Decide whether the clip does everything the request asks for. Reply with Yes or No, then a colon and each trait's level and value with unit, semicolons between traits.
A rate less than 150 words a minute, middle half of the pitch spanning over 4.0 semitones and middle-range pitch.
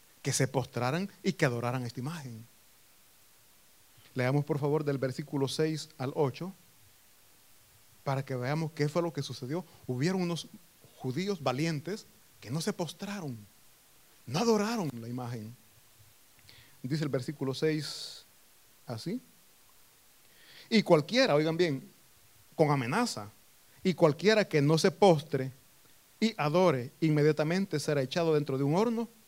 Yes: average, 125 wpm; average, 4.9 semitones; medium, 145 Hz